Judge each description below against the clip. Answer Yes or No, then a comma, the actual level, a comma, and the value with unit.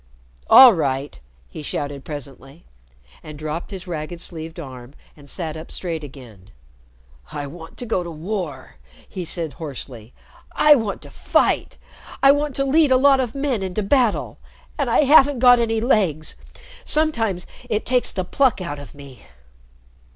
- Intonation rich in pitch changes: Yes, wide, 8.7 semitones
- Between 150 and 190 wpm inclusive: Yes, average, 160 wpm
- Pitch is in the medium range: Yes, medium, 175 Hz